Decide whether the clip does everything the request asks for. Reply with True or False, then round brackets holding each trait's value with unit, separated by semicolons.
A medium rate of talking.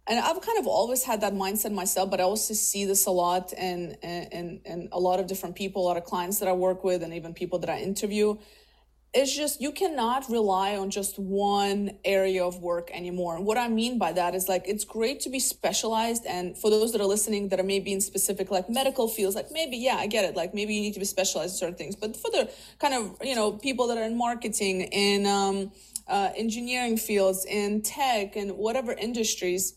False (235 wpm)